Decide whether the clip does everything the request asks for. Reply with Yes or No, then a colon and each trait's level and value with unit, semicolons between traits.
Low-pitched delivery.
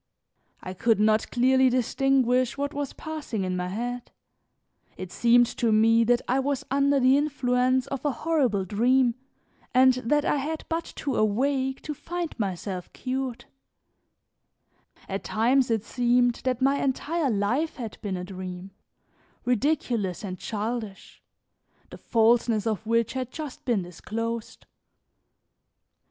No: high, 245 Hz